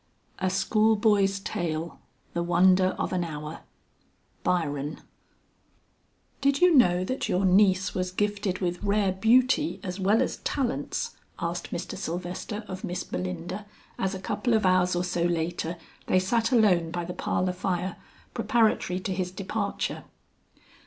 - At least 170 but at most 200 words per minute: No, average, 145 wpm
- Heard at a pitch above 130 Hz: Yes, medium, 185 Hz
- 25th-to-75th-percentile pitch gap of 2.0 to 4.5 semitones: Yes, average, 2.7 semitones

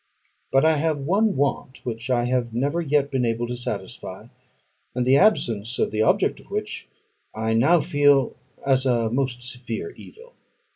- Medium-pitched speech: No, low, 130 Hz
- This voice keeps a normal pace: Yes, average, 165 wpm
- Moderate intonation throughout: Yes, average, 3.2 semitones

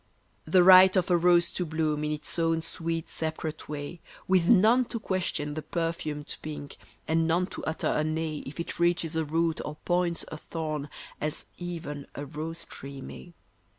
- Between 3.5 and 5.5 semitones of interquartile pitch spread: No, narrow, 2.4 semitones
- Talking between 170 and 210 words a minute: Yes, average, 180 wpm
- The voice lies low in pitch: No, medium, 165 Hz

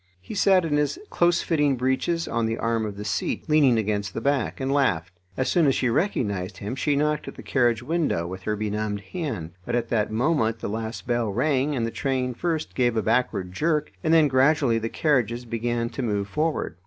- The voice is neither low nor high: No, low, 120 Hz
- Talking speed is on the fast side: Yes, fast, 210 wpm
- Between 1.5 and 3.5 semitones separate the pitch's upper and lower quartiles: No, average, 5.3 semitones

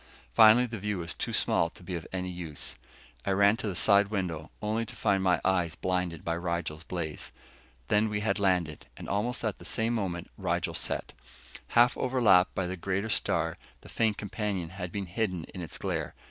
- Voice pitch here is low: Yes, very low, 95 Hz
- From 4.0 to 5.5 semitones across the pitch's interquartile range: No, average, 3.3 semitones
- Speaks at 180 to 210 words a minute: Yes, average, 195 wpm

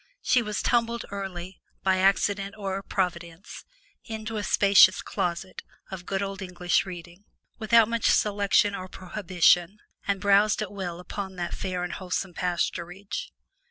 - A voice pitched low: No, high, 195 Hz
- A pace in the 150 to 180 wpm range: No, average, 140 wpm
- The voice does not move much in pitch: Yes, narrow, 2.3 semitones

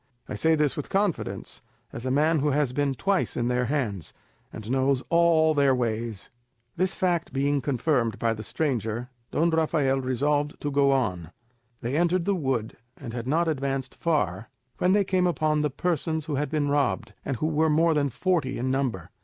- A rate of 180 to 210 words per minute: Yes, average, 185 wpm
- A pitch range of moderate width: Yes, average, 4.0 semitones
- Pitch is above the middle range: No, medium, 145 Hz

